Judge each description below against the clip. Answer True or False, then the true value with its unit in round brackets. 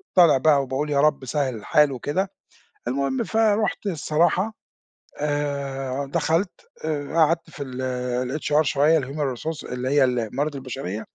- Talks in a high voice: False (145 Hz)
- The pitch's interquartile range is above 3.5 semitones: False (3.2 semitones)